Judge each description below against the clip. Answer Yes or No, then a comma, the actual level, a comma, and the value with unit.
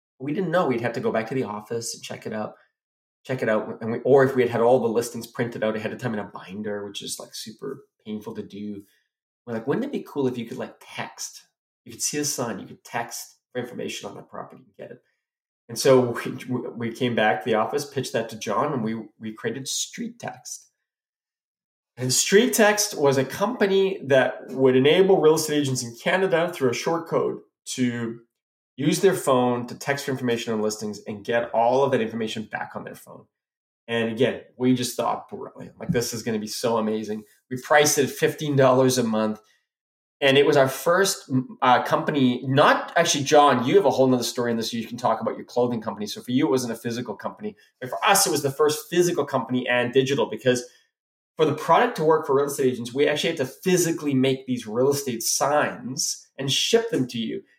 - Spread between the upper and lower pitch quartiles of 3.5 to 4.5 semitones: Yes, average, 4.1 semitones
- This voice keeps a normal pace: No, fast, 225 wpm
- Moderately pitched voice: No, low, 130 Hz